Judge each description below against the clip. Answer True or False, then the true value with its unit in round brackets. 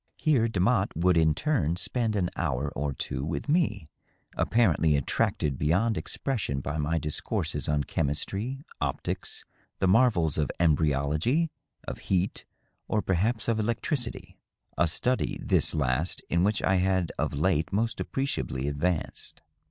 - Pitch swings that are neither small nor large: False (7.1 semitones)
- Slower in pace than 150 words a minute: True (140 wpm)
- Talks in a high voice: False (90 Hz)